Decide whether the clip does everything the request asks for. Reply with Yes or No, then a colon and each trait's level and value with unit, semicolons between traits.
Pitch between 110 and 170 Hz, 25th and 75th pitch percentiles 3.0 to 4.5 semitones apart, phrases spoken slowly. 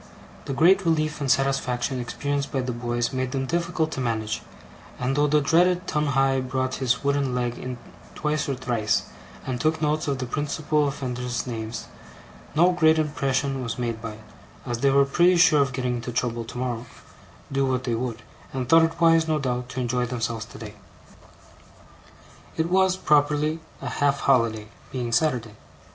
No: low, 135 Hz; average, 3.6 semitones; average, 170 wpm